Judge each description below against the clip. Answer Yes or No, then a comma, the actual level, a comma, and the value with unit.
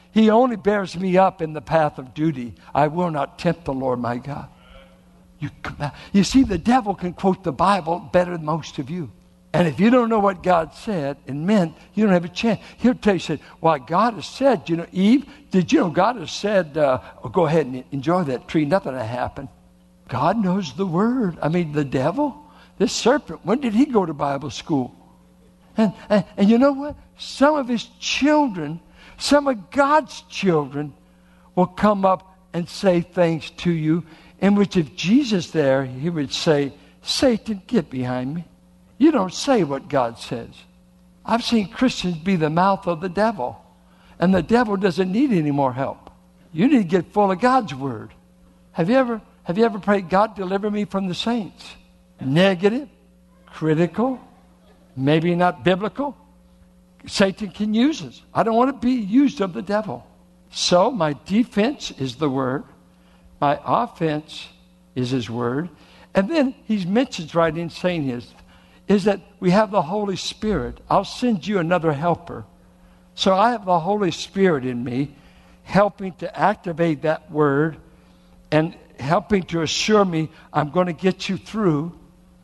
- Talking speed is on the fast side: No, average, 175 wpm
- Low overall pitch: No, medium, 175 Hz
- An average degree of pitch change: No, wide, 6.3 semitones